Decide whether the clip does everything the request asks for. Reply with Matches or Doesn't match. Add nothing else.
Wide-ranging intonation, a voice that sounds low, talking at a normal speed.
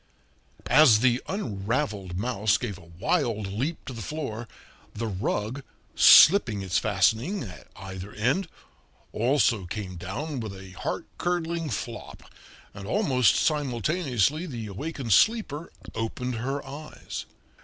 Doesn't match